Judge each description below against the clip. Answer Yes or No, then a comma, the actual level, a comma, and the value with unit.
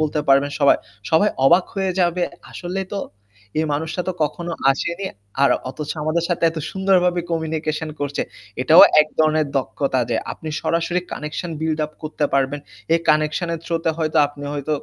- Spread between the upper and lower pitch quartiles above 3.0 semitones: No, narrow, 2.5 semitones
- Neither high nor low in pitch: Yes, medium, 160 Hz